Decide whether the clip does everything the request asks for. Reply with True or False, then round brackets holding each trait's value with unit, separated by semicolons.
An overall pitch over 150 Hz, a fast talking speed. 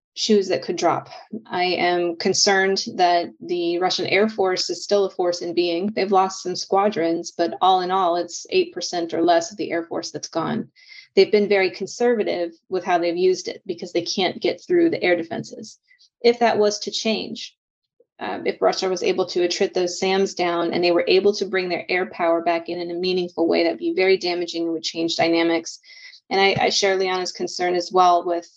True (185 Hz; 210 wpm)